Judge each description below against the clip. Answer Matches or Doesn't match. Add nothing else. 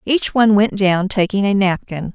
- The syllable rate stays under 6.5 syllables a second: Matches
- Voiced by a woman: Matches